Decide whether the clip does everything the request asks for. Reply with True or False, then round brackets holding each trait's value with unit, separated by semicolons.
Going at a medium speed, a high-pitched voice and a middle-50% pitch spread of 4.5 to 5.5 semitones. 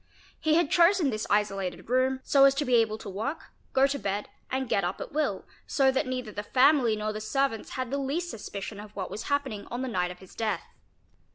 False (225 wpm; 245 Hz; 4.8 semitones)